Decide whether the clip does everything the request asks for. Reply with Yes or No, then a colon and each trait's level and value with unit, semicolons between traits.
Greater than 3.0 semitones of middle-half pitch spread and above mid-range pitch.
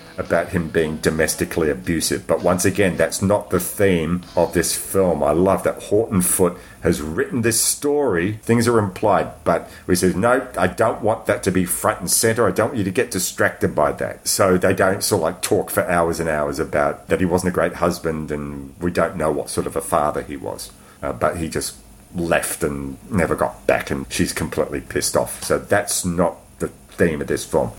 No: average, 3.5 semitones; very low, 90 Hz